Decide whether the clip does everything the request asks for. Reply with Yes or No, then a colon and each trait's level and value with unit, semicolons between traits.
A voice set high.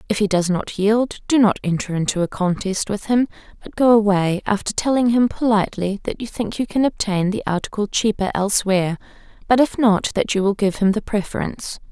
Yes: high, 205 Hz